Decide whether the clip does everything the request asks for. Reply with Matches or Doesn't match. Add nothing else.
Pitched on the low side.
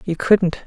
Doesn't match